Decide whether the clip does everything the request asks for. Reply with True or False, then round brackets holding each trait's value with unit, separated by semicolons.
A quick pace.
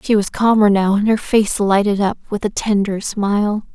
True (210 wpm)